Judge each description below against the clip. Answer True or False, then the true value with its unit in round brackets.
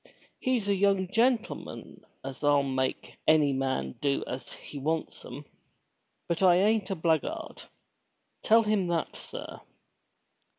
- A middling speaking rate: False (130 wpm)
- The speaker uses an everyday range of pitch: False (6.3 semitones)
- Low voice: False (170 Hz)